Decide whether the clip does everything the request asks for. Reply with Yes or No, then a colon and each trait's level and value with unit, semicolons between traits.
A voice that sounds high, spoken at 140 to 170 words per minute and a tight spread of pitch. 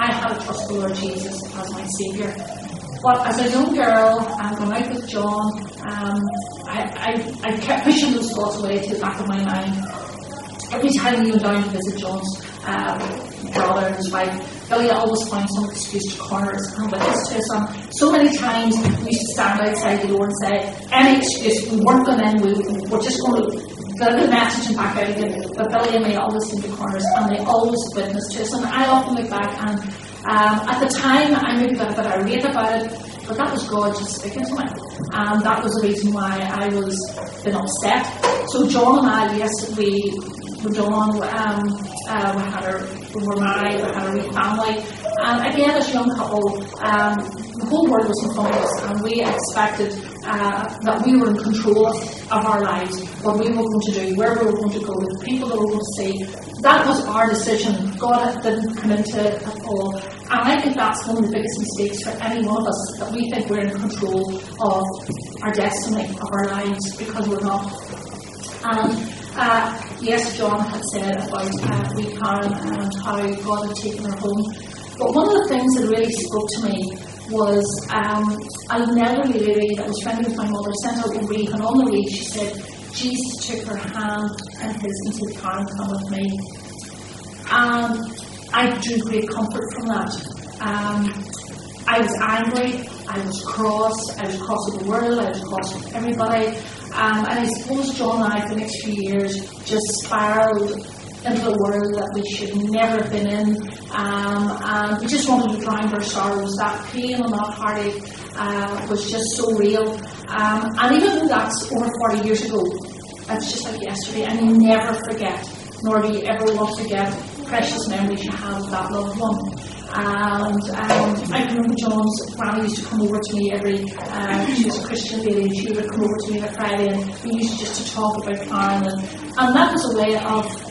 No: high, 215 Hz; fast, 205 wpm; narrow, 1.9 semitones